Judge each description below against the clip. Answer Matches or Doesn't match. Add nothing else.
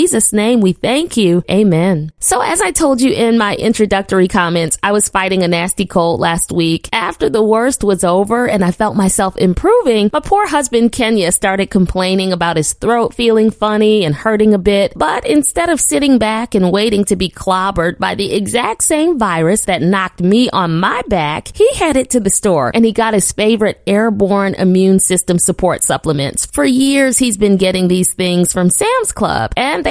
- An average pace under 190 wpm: Doesn't match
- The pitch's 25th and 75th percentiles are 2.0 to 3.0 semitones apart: Doesn't match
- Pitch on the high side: Matches